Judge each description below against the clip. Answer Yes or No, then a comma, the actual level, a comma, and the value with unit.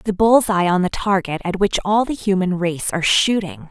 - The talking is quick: Yes, fast, 225 wpm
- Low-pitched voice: No, high, 190 Hz